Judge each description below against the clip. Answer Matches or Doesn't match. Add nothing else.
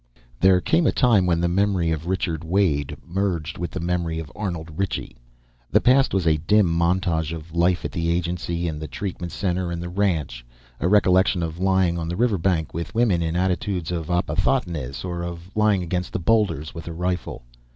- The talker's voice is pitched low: Matches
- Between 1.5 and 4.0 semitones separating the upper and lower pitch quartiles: Matches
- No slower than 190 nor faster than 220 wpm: Matches